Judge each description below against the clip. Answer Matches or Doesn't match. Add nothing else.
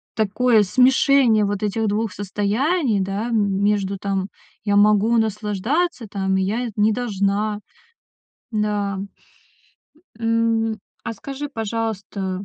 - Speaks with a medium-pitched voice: Doesn't match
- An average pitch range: Doesn't match